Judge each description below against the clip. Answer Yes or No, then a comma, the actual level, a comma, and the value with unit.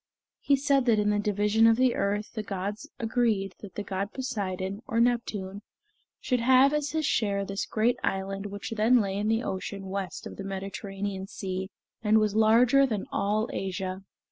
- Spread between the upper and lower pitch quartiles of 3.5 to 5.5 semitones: No, average, 2.9 semitones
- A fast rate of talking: No, average, 180 wpm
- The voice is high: Yes, high, 210 Hz